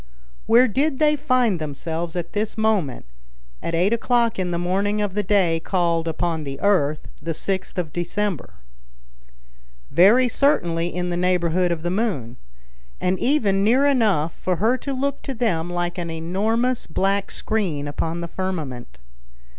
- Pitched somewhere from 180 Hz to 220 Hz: Yes, medium, 185 Hz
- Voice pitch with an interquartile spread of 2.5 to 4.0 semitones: No, average, 4.8 semitones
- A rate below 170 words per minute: Yes, average, 155 wpm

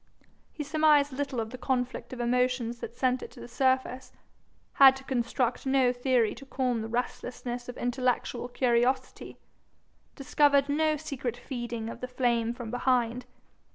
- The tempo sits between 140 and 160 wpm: Yes, average, 155 wpm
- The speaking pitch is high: Yes, very high, 250 Hz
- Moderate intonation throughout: No, narrow, 1.8 semitones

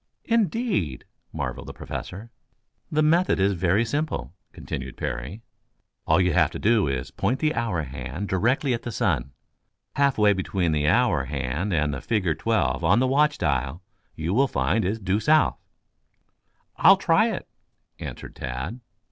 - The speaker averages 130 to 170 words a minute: Yes, average, 160 wpm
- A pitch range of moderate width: No, wide, 7.8 semitones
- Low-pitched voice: Yes, very low, 95 Hz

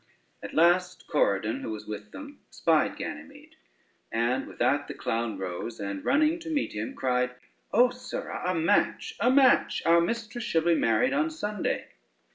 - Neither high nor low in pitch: Yes, medium, 170 Hz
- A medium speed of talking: Yes, average, 165 wpm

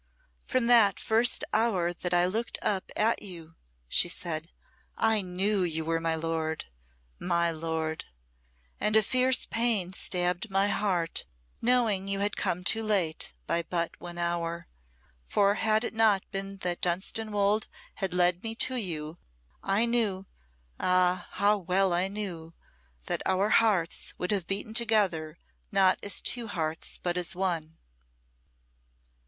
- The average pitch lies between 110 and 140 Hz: No, high, 190 Hz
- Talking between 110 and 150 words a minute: Yes, average, 145 wpm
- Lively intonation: No, average, 3.7 semitones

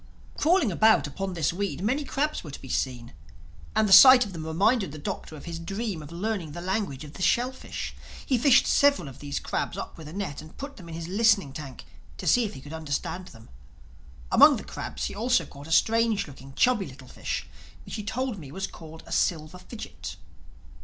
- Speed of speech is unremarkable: No, fast, 215 wpm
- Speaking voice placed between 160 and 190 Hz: Yes, medium, 185 Hz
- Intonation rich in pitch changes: Yes, wide, 6.5 semitones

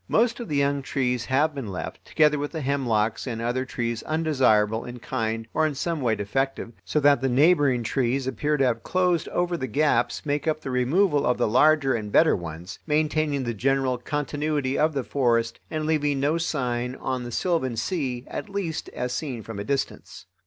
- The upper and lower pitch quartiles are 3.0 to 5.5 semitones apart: Yes, average, 4.0 semitones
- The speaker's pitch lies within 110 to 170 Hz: Yes, low, 135 Hz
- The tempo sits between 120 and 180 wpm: No, average, 195 wpm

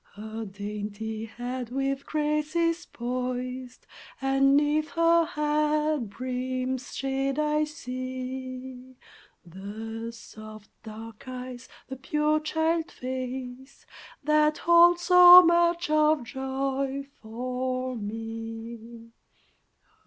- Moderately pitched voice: No, very high, 260 Hz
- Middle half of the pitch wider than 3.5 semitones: Yes, average, 4.4 semitones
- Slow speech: Yes, slow, 95 wpm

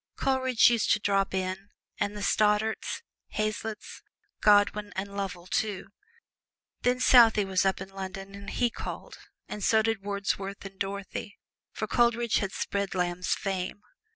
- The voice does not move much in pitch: Yes, narrow, 2.1 semitones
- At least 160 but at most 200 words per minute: No, average, 145 wpm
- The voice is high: Yes, high, 200 Hz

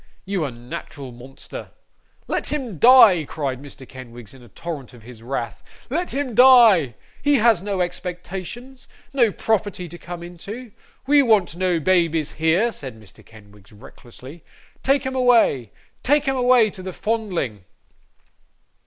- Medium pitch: Yes, medium, 180 Hz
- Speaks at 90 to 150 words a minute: Yes, average, 145 wpm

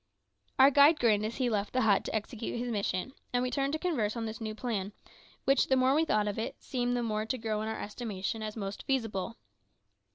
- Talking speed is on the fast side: Yes, fast, 230 wpm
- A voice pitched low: No, high, 225 Hz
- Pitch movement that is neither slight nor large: Yes, average, 3.3 semitones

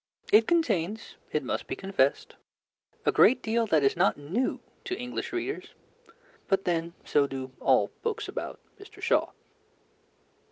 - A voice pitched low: No, high, 195 Hz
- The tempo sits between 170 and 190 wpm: No, average, 145 wpm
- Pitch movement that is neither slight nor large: No, wide, 8.4 semitones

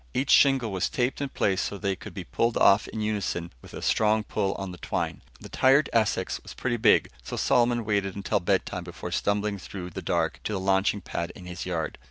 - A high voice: No, low, 100 Hz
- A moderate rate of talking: No, fast, 220 wpm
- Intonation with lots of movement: No, average, 3.3 semitones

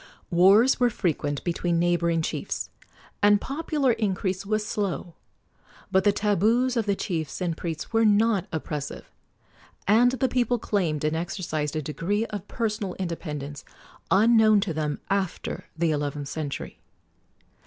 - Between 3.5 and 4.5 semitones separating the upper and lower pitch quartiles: No, average, 5.1 semitones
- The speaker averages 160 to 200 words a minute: No, slow, 135 wpm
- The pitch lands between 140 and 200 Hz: Yes, high, 190 Hz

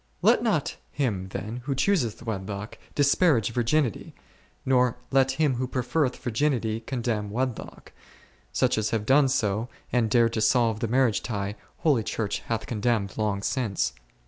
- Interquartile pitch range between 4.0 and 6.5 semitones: No, average, 3.4 semitones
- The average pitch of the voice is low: Yes, low, 115 Hz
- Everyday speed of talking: Yes, average, 150 wpm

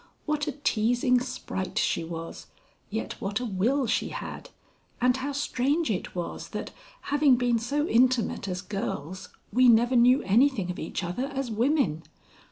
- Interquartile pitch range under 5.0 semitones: No, wide, 5.6 semitones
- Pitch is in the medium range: No, high, 245 Hz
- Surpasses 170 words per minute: No, average, 160 wpm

